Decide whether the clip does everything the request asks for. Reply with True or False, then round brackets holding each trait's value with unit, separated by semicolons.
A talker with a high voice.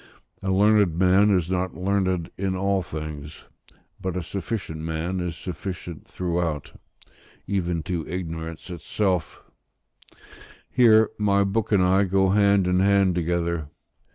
False (90 Hz)